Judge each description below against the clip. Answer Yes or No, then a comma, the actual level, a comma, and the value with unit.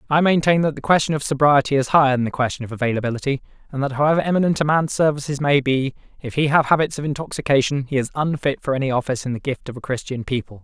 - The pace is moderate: No, fast, 235 wpm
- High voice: No, medium, 140 Hz